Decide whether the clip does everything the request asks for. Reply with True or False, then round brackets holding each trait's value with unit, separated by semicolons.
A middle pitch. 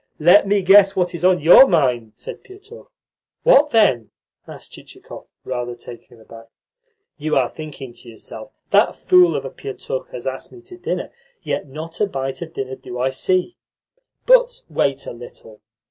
True (165 Hz)